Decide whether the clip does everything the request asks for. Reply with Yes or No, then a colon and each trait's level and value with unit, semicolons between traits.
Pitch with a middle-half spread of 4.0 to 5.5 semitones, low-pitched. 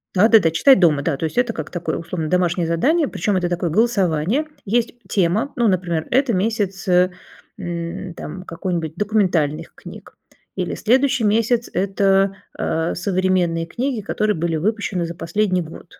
No: average, 4.4 semitones; medium, 185 Hz